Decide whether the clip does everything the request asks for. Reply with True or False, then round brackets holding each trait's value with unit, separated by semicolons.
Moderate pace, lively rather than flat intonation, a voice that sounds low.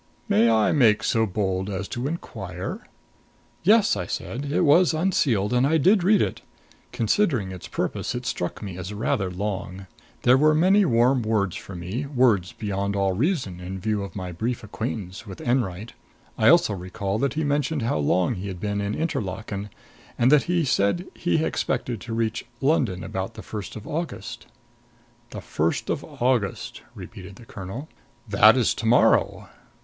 True (175 wpm; 6.2 semitones; 110 Hz)